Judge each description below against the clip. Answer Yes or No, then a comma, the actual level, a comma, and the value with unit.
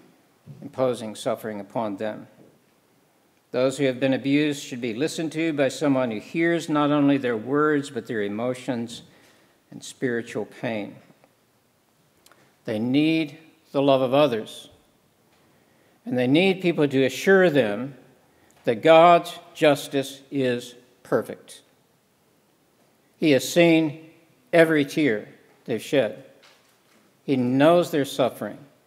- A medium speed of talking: No, slow, 115 wpm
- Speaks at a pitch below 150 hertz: Yes, medium, 140 Hz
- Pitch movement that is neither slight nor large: Yes, average, 3.8 semitones